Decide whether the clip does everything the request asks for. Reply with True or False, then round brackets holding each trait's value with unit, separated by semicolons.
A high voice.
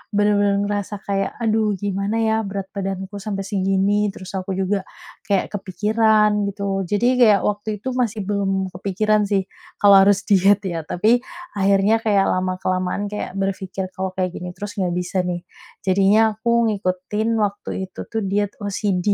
True (200 Hz)